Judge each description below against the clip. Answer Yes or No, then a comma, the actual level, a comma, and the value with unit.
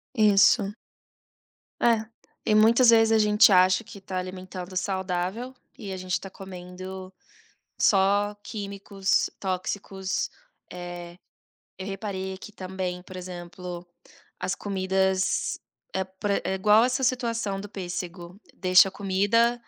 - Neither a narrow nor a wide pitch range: No, narrow, 2.0 semitones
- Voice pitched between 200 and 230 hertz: No, high, 190 Hz